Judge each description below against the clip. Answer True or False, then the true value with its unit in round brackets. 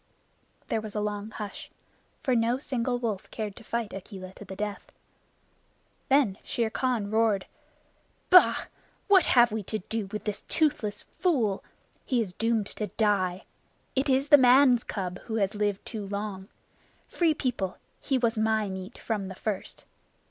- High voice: True (220 Hz)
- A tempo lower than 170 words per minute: True (160 wpm)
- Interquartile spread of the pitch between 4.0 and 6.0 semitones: False (3.3 semitones)